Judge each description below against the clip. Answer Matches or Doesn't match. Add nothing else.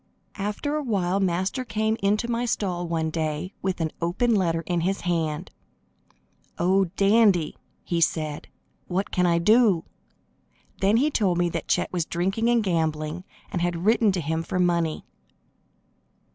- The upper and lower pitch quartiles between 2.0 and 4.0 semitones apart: Matches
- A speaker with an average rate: Matches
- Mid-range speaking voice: Matches